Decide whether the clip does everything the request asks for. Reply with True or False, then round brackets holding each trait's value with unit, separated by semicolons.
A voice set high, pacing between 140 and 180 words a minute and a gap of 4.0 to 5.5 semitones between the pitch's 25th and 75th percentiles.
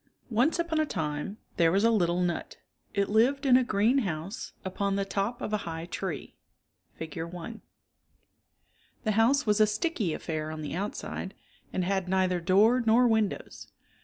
True (200 Hz; 165 wpm; 4.5 semitones)